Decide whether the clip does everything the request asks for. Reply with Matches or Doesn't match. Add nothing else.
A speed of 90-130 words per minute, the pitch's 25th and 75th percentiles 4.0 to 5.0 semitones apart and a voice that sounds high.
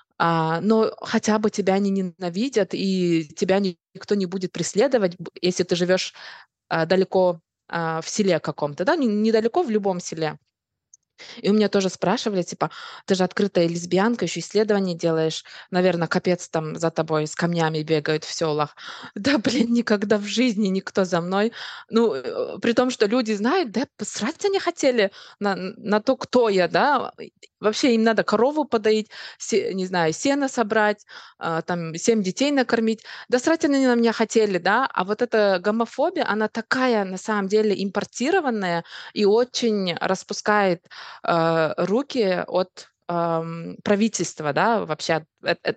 Doesn't match